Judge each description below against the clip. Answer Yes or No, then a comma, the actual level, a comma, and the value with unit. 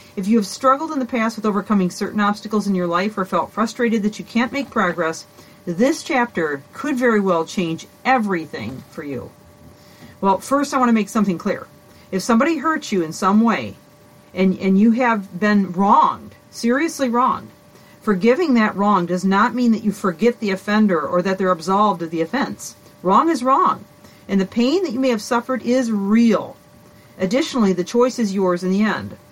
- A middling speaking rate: Yes, average, 190 wpm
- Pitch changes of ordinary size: Yes, average, 4.5 semitones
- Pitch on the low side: No, high, 210 Hz